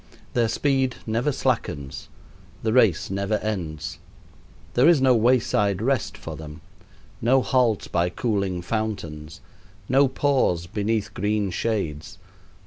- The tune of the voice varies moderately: No, wide, 5.8 semitones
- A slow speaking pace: Yes, slow, 120 wpm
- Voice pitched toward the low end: Yes, low, 110 Hz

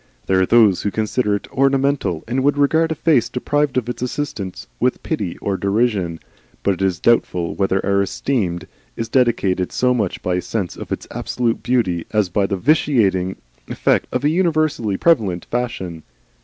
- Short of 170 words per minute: No, average, 175 wpm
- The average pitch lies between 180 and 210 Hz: No, low, 110 Hz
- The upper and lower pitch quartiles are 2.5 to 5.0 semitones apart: No, wide, 5.6 semitones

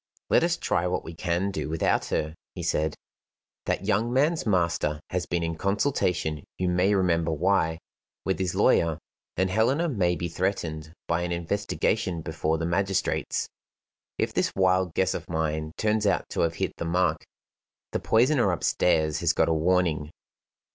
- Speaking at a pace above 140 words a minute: Yes, average, 165 wpm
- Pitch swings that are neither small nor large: Yes, average, 3.3 semitones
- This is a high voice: No, very low, 90 Hz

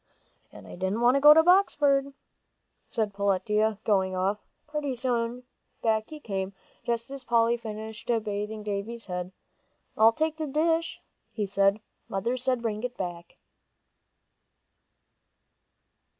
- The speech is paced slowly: Yes, slow, 130 wpm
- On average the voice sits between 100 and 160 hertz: No, high, 225 Hz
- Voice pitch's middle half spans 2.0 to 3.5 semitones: No, average, 4.5 semitones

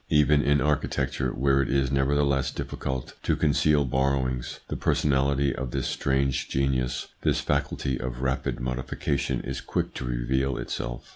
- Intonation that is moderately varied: No, narrow, 1.4 semitones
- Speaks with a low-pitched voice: Yes, very low, 65 Hz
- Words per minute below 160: Yes, average, 145 wpm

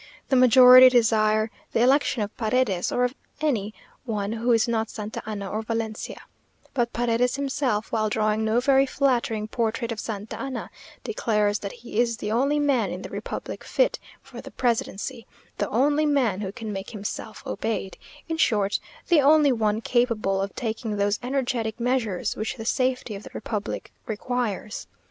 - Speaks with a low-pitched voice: No, high, 230 Hz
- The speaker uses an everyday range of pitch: Yes, average, 3.0 semitones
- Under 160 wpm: No, average, 165 wpm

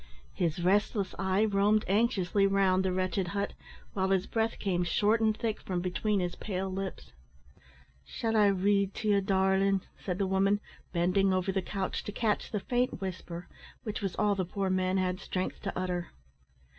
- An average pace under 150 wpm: No, average, 175 wpm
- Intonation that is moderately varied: No, narrow, 1.8 semitones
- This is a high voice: Yes, high, 195 Hz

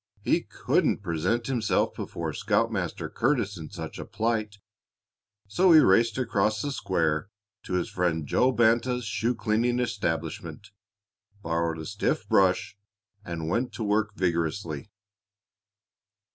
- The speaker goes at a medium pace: No, slow, 125 wpm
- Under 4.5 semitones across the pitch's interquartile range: No, wide, 5.5 semitones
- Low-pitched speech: Yes, low, 105 Hz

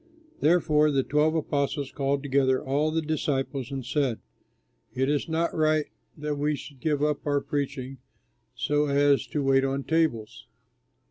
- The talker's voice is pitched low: No, medium, 145 Hz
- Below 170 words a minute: Yes, average, 150 wpm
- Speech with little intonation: Yes, narrow, 1.9 semitones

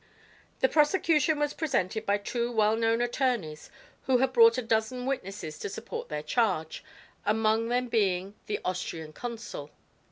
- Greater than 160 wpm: No, average, 150 wpm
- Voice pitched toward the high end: Yes, high, 225 Hz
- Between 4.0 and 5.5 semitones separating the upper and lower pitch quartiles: Yes, average, 4.3 semitones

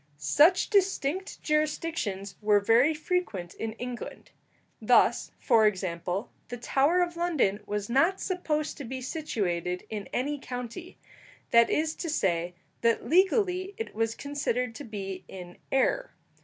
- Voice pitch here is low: No, very high, 250 Hz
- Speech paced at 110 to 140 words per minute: Yes, slow, 135 wpm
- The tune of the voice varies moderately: No, wide, 8.1 semitones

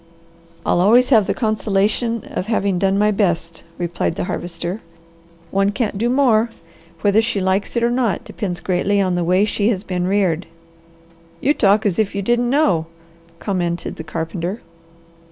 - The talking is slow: No, average, 165 wpm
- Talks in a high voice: Yes, high, 200 Hz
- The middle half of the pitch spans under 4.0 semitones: Yes, average, 3.6 semitones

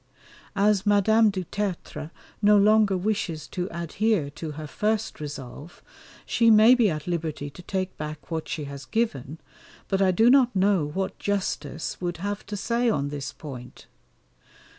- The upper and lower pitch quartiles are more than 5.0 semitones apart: Yes, wide, 5.4 semitones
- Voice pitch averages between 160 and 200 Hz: Yes, medium, 185 Hz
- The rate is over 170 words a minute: No, average, 160 wpm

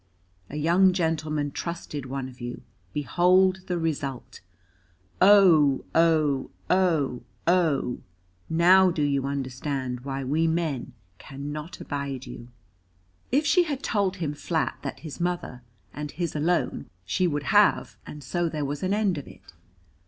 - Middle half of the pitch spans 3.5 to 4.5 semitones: Yes, average, 4.2 semitones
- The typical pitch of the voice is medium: Yes, medium, 155 Hz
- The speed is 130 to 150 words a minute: Yes, average, 140 wpm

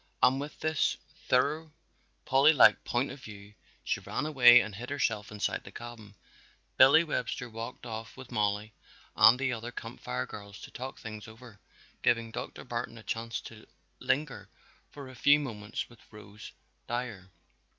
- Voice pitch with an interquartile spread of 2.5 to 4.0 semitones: Yes, average, 3.4 semitones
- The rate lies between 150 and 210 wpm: Yes, average, 160 wpm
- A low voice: Yes, low, 120 Hz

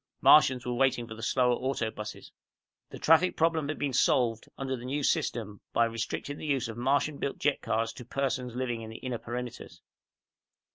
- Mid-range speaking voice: No, low, 125 Hz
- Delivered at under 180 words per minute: No, average, 195 wpm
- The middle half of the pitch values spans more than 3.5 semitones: No, average, 3.0 semitones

